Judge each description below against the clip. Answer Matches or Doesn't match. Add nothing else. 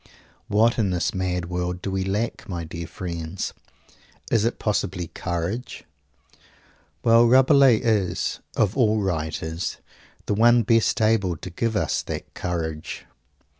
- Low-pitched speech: Matches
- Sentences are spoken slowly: Matches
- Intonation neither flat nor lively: Matches